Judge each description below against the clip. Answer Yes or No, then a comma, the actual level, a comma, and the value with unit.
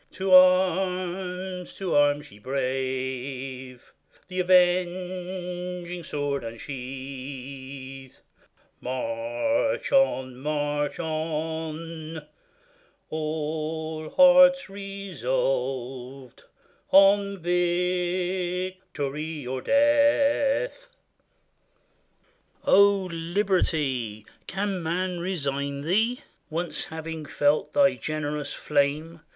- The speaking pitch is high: No, medium, 165 Hz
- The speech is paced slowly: Yes, slow, 65 wpm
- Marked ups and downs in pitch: No, average, 4.8 semitones